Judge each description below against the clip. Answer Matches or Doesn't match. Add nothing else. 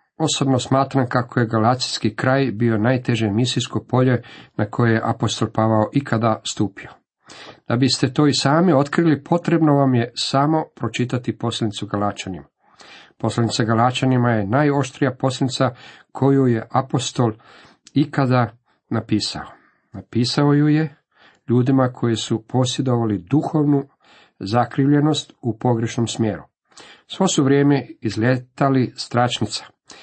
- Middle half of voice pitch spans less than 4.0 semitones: Matches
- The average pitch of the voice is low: Matches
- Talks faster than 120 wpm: Doesn't match